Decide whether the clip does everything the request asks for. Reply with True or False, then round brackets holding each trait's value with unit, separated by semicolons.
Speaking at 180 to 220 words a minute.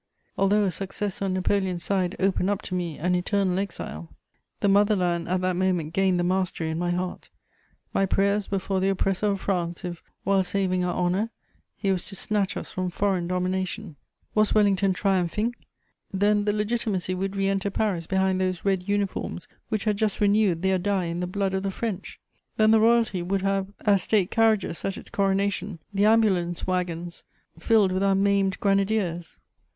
True (185 wpm)